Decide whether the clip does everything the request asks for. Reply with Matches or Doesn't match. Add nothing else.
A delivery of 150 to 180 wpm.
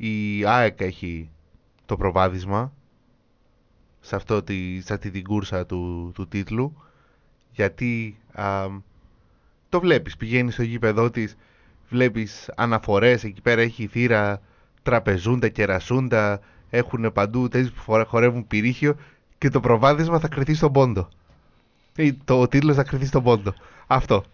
Doesn't match